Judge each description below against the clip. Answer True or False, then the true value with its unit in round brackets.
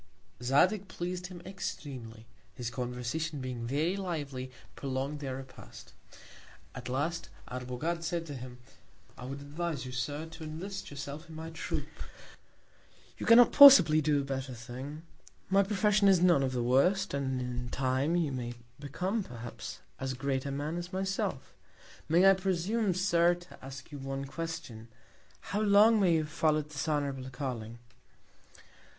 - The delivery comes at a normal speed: True (155 wpm)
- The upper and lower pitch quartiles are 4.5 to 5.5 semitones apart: True (5.1 semitones)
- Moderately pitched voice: True (150 Hz)